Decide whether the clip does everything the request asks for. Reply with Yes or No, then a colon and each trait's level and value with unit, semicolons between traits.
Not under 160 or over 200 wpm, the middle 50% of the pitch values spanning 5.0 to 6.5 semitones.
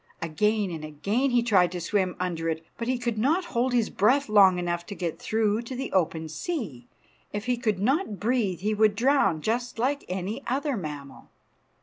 Yes: average, 195 wpm; wide, 5.5 semitones